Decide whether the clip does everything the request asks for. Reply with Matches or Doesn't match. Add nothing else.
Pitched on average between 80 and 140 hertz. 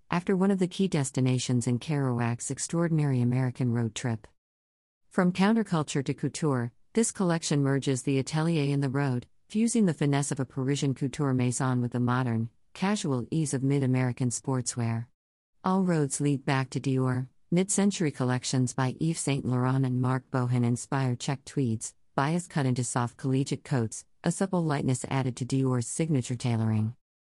Matches